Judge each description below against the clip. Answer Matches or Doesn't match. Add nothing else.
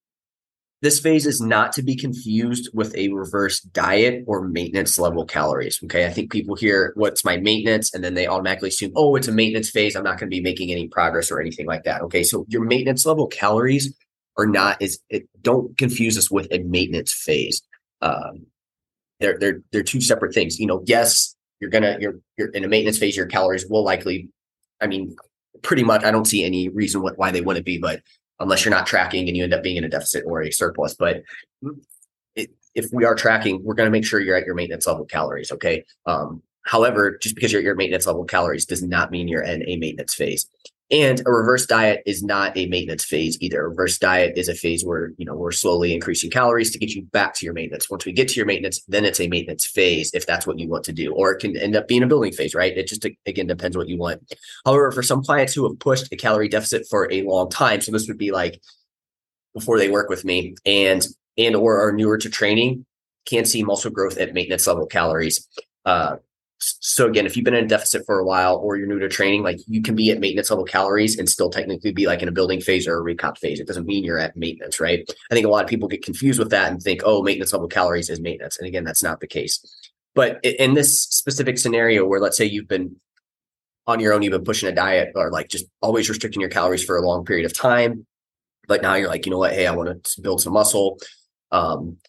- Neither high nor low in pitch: Doesn't match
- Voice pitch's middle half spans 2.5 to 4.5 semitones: Matches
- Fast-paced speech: Matches